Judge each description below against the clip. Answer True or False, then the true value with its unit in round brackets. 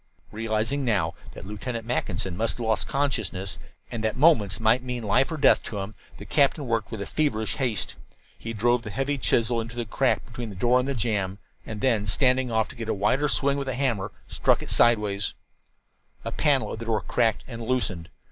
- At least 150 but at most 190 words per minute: False (205 wpm)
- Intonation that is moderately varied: True (3.3 semitones)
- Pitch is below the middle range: True (115 Hz)